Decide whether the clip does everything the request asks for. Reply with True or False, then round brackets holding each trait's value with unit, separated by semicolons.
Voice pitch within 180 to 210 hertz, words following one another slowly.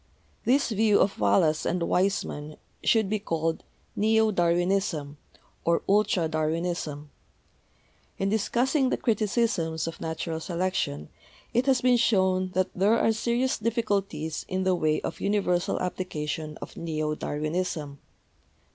True (185 Hz; 130 wpm)